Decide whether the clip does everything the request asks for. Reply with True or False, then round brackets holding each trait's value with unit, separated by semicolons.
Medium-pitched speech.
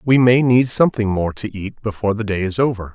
False (110 Hz)